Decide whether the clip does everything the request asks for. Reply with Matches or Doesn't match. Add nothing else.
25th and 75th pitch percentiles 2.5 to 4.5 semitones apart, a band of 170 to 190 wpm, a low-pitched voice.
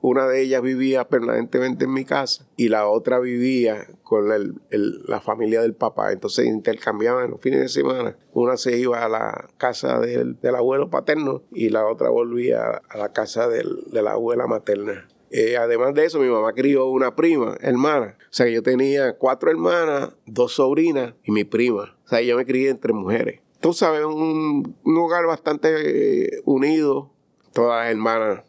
Doesn't match